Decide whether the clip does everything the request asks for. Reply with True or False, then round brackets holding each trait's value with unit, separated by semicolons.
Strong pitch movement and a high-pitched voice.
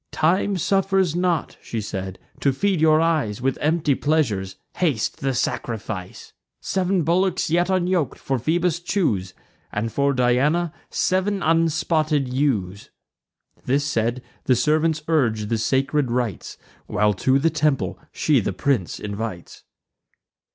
False (6.5 semitones; 145 Hz)